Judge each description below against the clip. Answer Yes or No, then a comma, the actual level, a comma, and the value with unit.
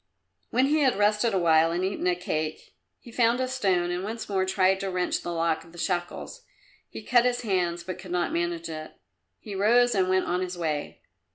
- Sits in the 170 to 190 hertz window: Yes, medium, 185 Hz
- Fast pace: Yes, fast, 215 wpm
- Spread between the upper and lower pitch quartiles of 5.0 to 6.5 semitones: No, average, 4.0 semitones